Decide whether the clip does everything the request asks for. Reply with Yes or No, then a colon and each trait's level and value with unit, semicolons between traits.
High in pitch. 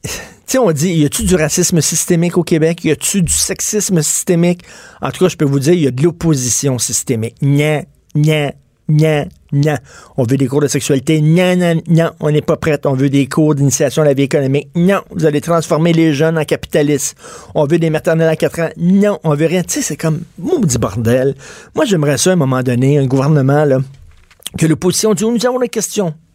No: medium, 155 Hz